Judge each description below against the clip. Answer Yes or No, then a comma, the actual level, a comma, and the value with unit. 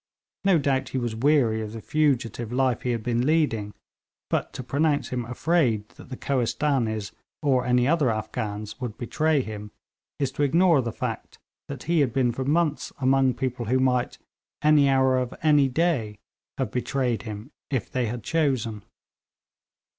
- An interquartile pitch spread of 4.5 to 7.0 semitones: No, average, 3.7 semitones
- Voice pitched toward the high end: No, low, 130 Hz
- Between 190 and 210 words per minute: No, average, 165 wpm